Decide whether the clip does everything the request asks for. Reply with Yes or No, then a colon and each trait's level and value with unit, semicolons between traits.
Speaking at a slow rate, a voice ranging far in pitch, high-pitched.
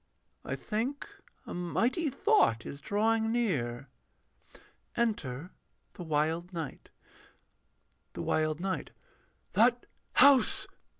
Yes: slow, 95 wpm; wide, 7.3 semitones; high, 195 Hz